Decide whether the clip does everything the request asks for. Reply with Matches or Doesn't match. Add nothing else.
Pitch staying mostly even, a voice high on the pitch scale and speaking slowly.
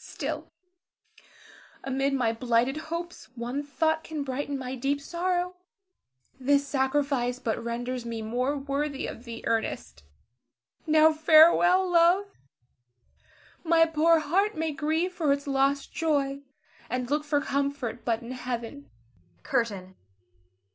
Doesn't match